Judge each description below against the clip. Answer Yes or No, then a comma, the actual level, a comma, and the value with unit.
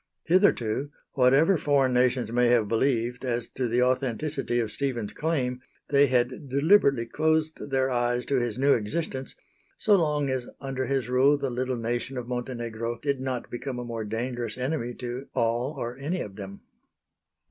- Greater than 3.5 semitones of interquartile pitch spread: No, narrow, 2.6 semitones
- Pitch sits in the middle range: No, low, 125 Hz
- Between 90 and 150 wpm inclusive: No, average, 165 wpm